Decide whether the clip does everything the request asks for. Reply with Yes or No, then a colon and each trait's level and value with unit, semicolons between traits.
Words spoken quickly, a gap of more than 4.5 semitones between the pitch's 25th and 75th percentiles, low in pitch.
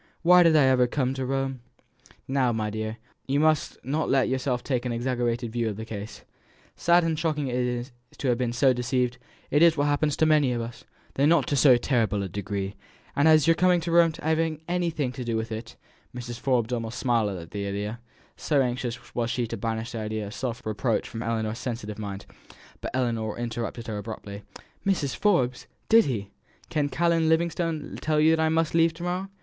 Yes: fast, 210 wpm; average, 5.2 semitones; low, 125 Hz